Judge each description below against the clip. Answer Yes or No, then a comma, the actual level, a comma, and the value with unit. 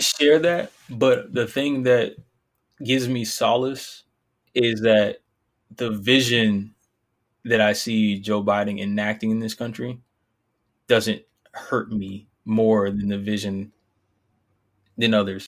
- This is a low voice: Yes, low, 110 Hz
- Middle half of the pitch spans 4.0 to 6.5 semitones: No, average, 2.7 semitones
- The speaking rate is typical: No, slow, 120 wpm